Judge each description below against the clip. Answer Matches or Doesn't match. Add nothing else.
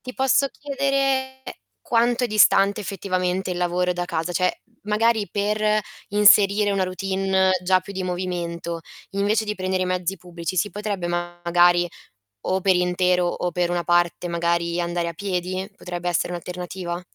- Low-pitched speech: Doesn't match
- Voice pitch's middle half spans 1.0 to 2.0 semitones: Doesn't match